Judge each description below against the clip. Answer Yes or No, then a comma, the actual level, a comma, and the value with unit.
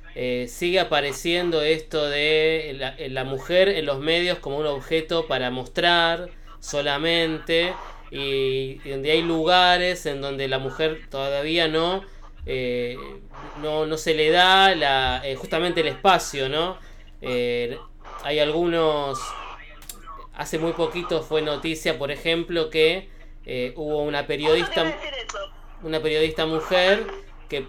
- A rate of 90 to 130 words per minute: Yes, slow, 125 wpm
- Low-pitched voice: No, medium, 155 Hz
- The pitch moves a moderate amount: Yes, average, 3.3 semitones